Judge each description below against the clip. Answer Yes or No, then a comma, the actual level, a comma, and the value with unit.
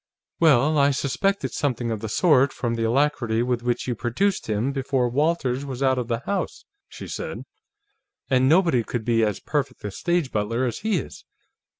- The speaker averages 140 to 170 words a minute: No, average, 185 wpm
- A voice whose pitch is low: Yes, low, 130 Hz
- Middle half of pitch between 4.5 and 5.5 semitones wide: No, average, 3.7 semitones